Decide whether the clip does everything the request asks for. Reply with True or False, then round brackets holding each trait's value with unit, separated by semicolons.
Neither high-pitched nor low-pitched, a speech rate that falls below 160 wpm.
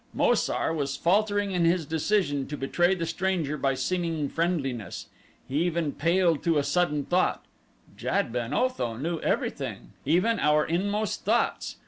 True (165 Hz; 150 wpm)